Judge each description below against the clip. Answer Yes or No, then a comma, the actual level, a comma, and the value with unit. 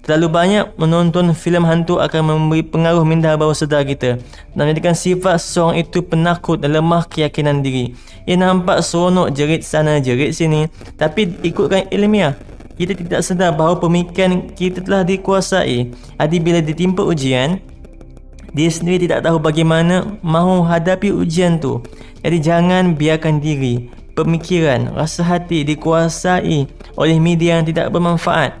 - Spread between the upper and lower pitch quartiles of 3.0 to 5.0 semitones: No, narrow, 2.5 semitones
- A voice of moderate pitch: Yes, medium, 165 Hz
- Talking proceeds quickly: No, average, 140 wpm